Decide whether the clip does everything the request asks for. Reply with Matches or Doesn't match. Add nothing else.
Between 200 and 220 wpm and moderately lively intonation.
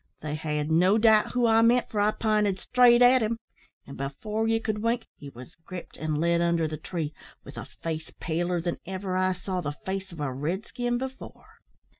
Doesn't match